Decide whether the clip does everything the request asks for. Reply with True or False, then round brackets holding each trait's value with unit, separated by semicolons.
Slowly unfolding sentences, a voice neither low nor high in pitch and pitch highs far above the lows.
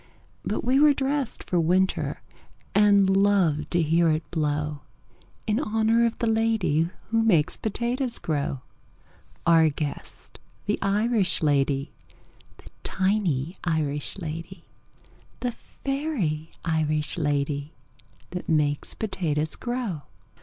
True (110 wpm; 175 Hz; 6.4 semitones)